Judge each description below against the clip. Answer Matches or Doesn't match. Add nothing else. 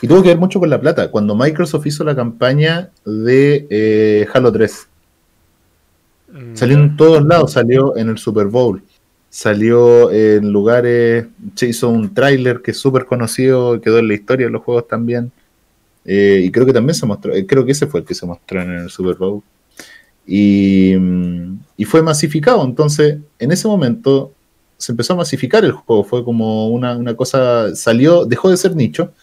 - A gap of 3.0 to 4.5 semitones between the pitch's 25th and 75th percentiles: Doesn't match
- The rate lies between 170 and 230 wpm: Matches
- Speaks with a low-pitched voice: Matches